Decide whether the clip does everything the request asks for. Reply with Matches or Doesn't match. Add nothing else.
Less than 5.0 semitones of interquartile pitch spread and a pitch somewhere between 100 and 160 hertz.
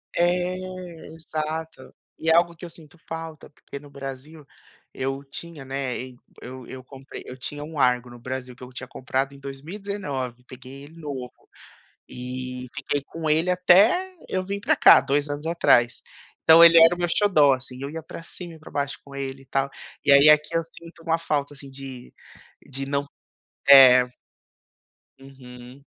Matches